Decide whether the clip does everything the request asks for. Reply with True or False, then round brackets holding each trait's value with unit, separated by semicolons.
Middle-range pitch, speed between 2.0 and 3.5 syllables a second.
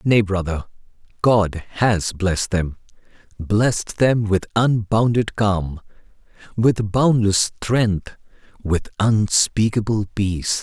False (105 Hz; 3.4 syllables/s)